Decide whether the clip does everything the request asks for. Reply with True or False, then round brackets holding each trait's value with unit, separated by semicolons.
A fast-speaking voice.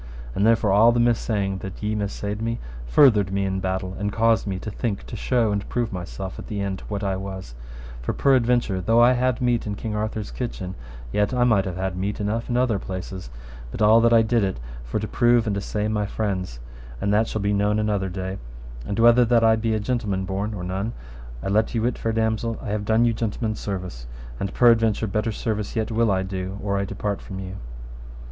True (220 wpm)